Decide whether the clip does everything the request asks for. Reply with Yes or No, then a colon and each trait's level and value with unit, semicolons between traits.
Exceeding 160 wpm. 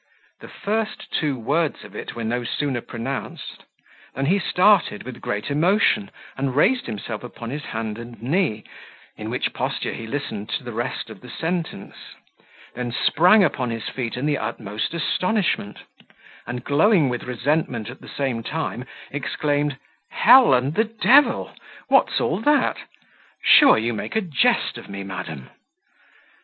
No: average, 155 wpm